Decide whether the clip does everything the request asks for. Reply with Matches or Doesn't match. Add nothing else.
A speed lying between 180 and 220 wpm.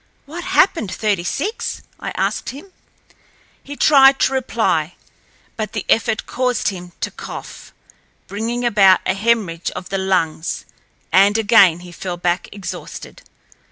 Doesn't match